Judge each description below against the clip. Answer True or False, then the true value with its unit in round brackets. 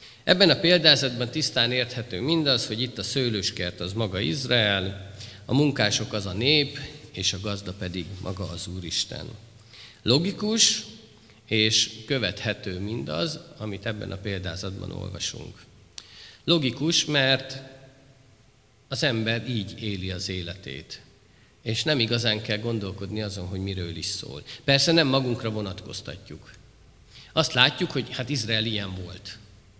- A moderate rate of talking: True (125 wpm)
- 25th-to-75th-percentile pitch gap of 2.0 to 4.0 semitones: False (5.1 semitones)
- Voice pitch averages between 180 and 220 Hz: False (110 Hz)